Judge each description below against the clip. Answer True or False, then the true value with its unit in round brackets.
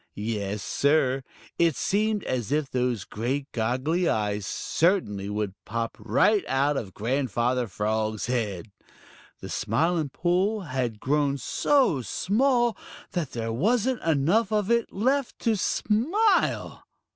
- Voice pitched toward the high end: False (140 Hz)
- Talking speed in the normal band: False (120 wpm)